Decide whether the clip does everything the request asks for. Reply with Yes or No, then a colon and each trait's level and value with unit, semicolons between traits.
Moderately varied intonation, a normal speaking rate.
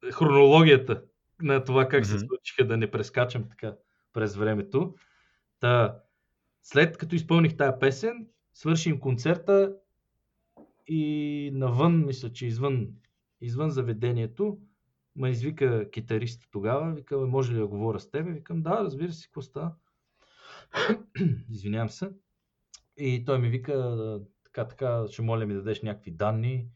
No: wide, 5.9 semitones; average, 130 wpm